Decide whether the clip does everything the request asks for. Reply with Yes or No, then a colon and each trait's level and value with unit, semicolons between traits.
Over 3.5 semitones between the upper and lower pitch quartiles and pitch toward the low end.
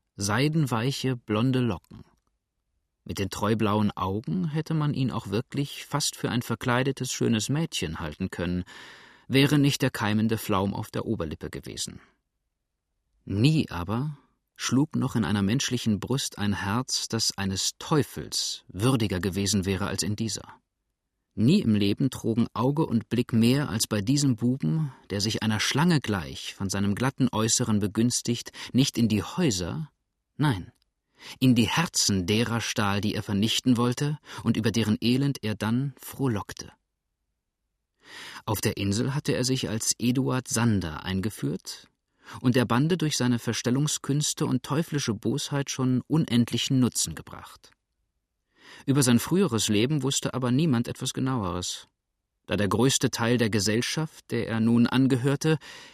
Yes: average, 4.1 semitones; low, 120 Hz